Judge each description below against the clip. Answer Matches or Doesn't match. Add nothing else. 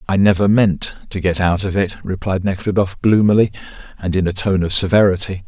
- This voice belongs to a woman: Doesn't match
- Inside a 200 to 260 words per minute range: Doesn't match